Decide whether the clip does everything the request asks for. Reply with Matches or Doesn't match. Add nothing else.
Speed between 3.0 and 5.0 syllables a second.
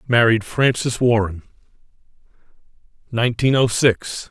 Matches